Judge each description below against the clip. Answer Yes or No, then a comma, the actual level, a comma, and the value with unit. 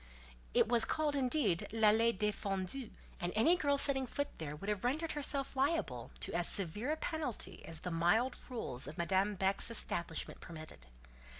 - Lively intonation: Yes, wide, 7.7 semitones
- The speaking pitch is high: Yes, high, 215 Hz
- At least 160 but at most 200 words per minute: Yes, average, 165 wpm